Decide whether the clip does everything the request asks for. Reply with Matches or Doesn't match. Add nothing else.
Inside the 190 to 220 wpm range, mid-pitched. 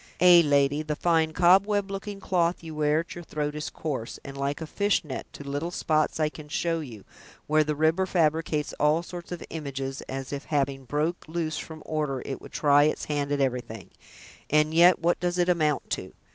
Matches